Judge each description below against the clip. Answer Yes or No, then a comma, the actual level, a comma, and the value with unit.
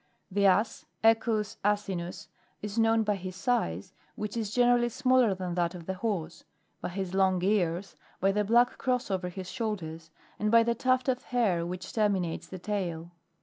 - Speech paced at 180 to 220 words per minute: Yes, average, 185 wpm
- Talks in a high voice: Yes, high, 200 Hz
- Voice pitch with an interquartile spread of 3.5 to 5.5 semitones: Yes, average, 4.0 semitones